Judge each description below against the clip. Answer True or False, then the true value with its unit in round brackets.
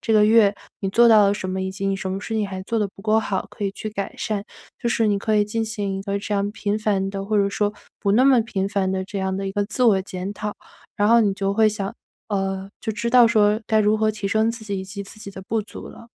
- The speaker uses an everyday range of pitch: False (1.8 semitones)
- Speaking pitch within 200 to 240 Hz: True (205 Hz)